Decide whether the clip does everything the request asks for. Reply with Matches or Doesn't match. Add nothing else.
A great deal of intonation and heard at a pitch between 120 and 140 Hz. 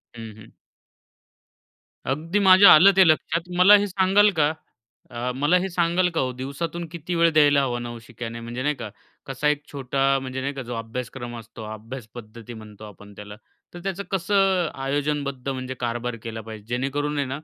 Matches